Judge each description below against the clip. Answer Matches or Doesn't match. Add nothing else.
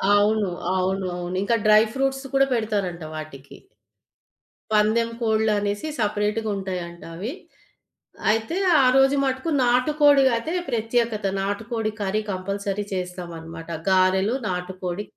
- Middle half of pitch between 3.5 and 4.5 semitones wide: Matches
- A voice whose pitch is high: Matches